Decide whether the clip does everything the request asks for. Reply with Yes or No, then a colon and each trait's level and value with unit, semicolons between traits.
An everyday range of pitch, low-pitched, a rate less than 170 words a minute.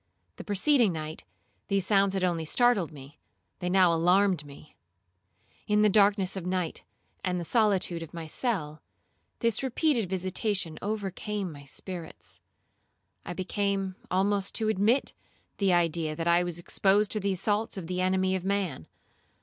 No: average, 3.0 semitones; high, 190 Hz; average, 150 wpm